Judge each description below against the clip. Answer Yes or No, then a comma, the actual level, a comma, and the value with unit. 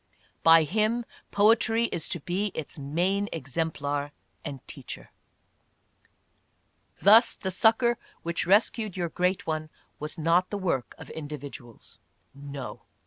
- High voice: No, medium, 170 Hz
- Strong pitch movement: Yes, wide, 5.7 semitones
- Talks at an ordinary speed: No, slow, 120 wpm